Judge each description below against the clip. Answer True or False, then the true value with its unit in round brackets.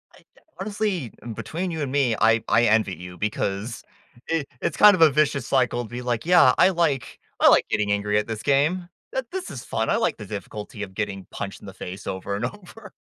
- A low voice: True (120 Hz)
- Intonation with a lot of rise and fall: True (7.6 semitones)